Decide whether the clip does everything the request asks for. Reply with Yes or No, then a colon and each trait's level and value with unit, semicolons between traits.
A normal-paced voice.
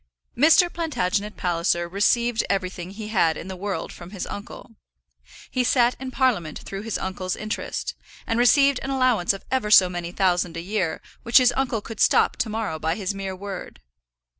Yes: average, 180 wpm